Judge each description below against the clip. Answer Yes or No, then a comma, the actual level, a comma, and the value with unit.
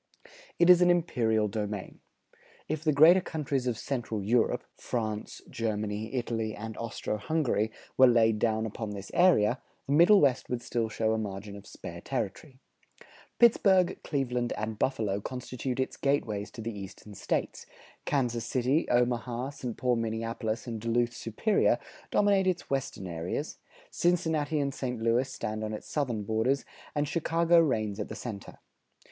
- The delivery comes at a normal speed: Yes, average, 150 wpm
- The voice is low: Yes, low, 120 Hz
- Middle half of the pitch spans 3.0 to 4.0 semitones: No, average, 4.6 semitones